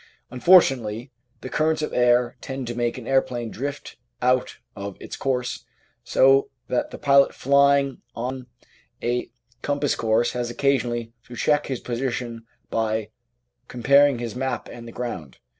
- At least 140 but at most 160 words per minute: Yes, average, 145 wpm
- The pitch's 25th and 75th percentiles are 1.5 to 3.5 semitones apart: Yes, narrow, 2.5 semitones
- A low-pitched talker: Yes, low, 125 Hz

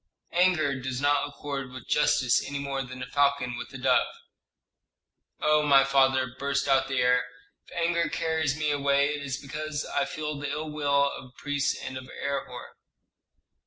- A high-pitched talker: No, medium, 140 Hz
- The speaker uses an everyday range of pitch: No, narrow, 2.0 semitones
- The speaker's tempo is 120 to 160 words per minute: No, average, 175 wpm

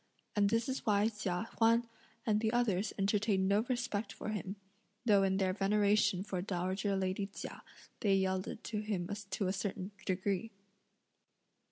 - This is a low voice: No, high, 200 Hz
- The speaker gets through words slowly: No, average, 155 wpm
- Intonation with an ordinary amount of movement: No, narrow, 2.1 semitones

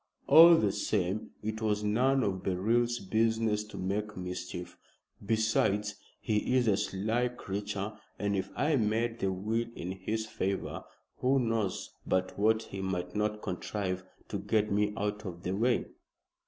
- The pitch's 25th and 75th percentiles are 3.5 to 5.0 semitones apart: No, narrow, 2.6 semitones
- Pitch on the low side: Yes, low, 105 Hz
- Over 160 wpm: No, average, 155 wpm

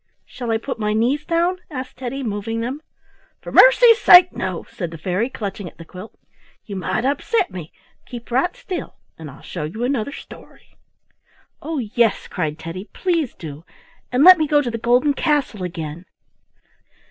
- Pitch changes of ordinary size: No, wide, 7.6 semitones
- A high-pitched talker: Yes, high, 240 Hz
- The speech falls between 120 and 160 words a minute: No, average, 170 wpm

